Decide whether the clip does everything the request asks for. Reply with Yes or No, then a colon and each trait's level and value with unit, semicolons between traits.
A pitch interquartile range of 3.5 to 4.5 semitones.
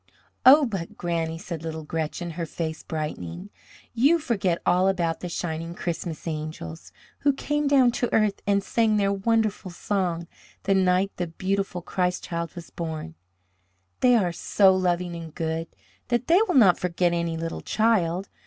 Yes: average, 3.8 semitones